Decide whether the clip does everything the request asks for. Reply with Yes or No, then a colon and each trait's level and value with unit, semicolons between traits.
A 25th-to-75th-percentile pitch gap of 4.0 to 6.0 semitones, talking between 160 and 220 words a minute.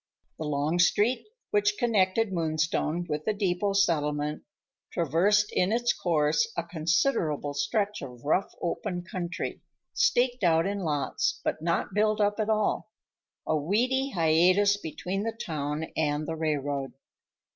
No: average, 5.0 semitones; slow, 135 wpm